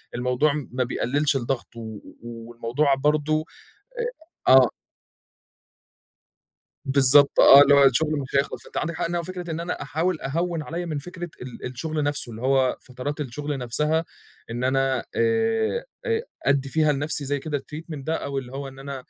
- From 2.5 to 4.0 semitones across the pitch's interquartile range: Yes, average, 3.3 semitones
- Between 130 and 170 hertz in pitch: Yes, medium, 140 Hz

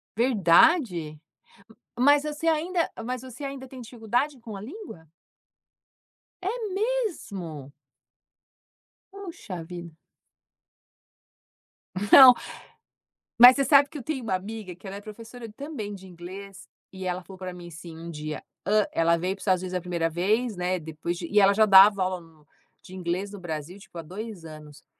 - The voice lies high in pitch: Yes, high, 195 Hz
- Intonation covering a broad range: Yes, wide, 6.3 semitones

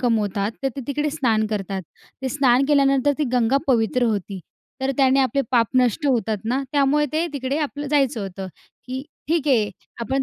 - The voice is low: No, very high, 260 Hz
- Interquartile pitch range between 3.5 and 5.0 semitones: Yes, average, 4.0 semitones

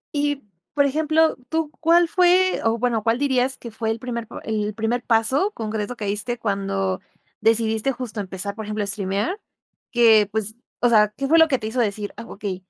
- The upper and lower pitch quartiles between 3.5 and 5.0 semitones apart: Yes, average, 4.3 semitones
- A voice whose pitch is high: Yes, high, 225 Hz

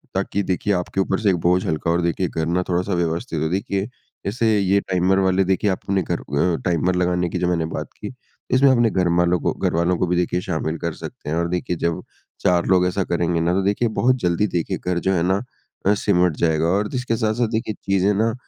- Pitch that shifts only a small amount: Yes, narrow, 2.3 semitones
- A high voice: No, very low, 90 Hz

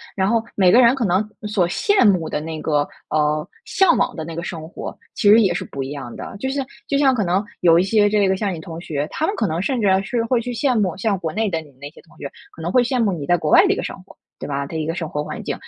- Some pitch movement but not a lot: No, wide, 6.2 semitones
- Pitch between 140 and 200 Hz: Yes, medium, 185 Hz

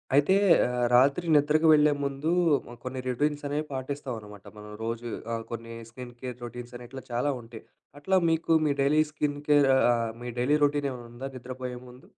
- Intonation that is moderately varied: Yes, average, 3.2 semitones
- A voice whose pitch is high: No, low, 130 Hz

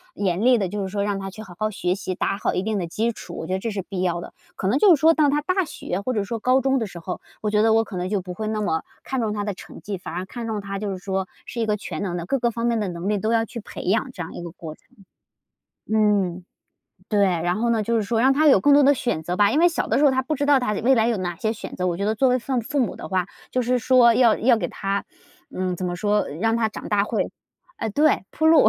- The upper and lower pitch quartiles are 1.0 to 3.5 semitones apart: No, average, 4.0 semitones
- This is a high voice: Yes, high, 210 Hz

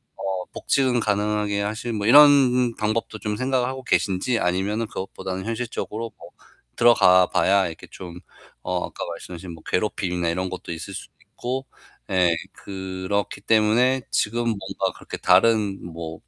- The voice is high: No, low, 105 Hz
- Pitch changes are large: No, average, 3.9 semitones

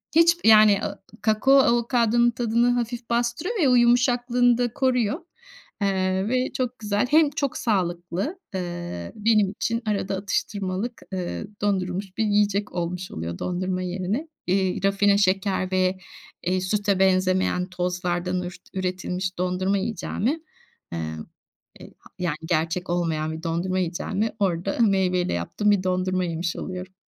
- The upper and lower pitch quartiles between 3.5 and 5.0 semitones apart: Yes, average, 4.0 semitones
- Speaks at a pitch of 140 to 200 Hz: Yes, high, 190 Hz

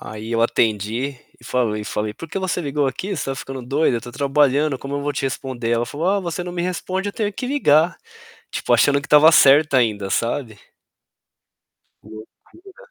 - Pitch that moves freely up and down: Yes, wide, 5.8 semitones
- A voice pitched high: No, medium, 140 Hz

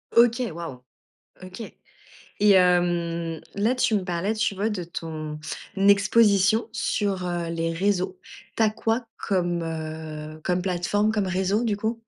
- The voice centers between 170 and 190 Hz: Yes, medium, 185 Hz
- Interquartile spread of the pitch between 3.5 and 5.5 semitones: Yes, average, 3.8 semitones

